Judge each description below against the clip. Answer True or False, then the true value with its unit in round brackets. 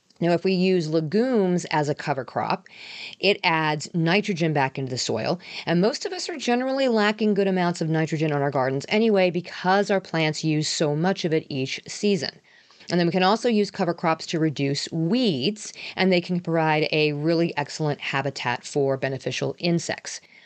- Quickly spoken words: False (185 wpm)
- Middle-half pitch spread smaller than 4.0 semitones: False (4.6 semitones)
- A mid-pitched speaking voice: True (170 Hz)